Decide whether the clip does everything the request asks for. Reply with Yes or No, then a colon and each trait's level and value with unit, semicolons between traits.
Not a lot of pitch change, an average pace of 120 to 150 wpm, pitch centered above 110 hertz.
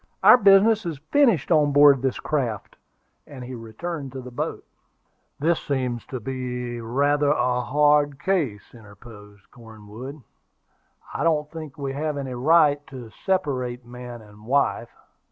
No: average, 3.6 semitones; average, 145 wpm; low, 135 Hz